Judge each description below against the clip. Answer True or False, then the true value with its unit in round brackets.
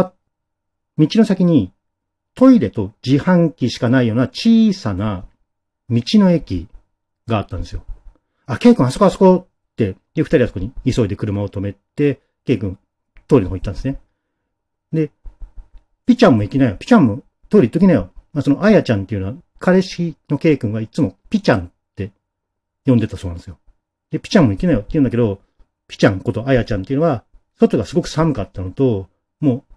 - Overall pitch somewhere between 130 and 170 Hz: False (110 Hz)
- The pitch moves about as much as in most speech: False (7.2 semitones)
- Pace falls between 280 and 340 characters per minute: False (380 characters per minute)